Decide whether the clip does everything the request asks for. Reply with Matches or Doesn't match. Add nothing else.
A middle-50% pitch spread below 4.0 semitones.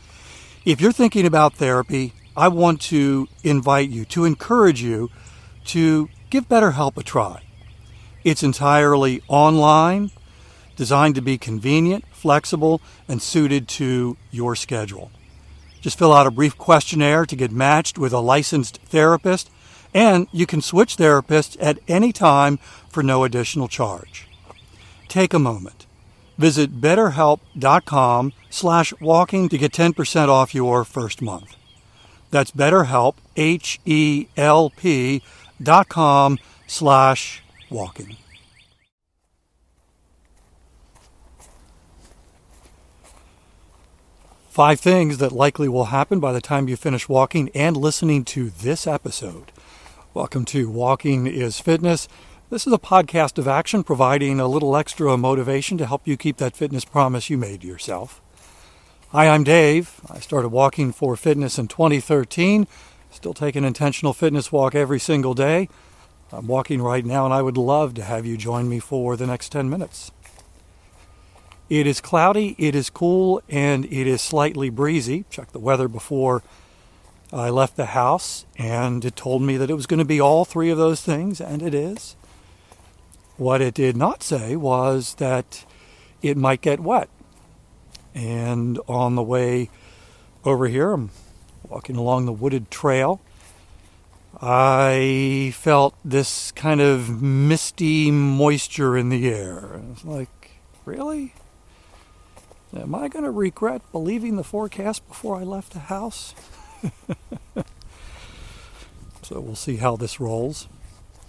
Doesn't match